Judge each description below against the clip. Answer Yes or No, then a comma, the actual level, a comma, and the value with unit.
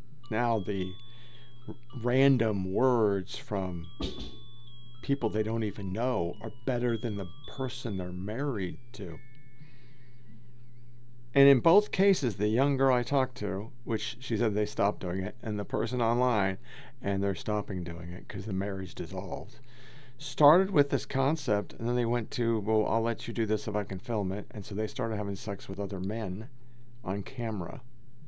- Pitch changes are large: No, average, 3.6 semitones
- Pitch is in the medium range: No, low, 115 Hz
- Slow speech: No, average, 170 wpm